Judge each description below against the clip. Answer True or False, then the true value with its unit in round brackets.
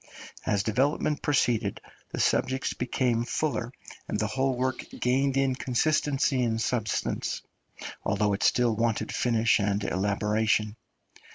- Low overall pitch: True (120 Hz)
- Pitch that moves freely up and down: False (3.5 semitones)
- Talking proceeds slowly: True (120 wpm)